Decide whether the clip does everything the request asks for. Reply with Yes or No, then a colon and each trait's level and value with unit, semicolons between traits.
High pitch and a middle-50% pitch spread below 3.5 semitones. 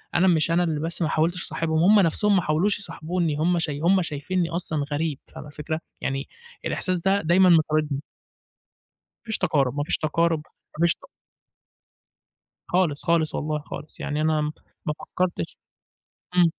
No: medium, 165 Hz; average, 2.8 semitones